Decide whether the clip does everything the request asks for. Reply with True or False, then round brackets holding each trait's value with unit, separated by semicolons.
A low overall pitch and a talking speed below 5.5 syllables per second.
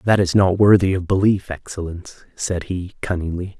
True (95 Hz; 5.1 syllables/s)